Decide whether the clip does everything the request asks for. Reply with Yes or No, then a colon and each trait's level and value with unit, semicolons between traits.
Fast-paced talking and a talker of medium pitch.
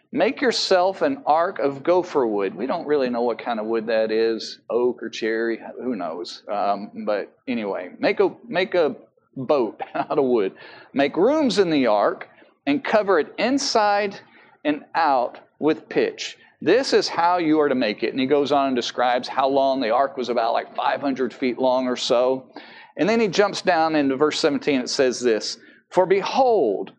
No: average, 190 wpm; medium, 155 Hz